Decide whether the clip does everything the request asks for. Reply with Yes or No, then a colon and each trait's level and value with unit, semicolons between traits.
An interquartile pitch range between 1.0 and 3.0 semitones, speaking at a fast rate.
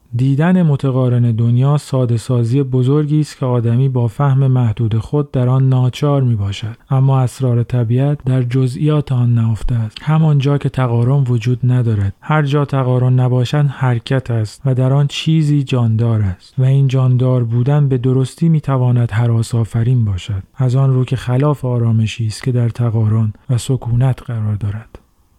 Yes: narrow, 2.5 semitones; fast, 160 wpm